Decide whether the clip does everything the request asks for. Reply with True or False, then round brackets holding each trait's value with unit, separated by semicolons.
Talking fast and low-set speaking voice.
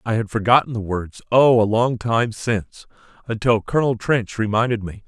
False (155 wpm; 110 Hz)